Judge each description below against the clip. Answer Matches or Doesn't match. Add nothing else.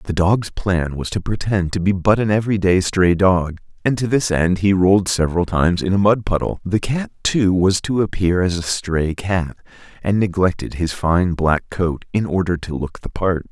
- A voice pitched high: Doesn't match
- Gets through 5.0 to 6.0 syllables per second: Doesn't match